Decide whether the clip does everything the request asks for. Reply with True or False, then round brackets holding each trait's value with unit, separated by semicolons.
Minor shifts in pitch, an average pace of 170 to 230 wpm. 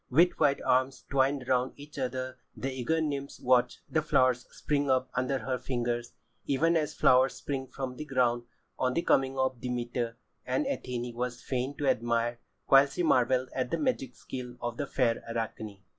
True (2.0 semitones; 185 wpm)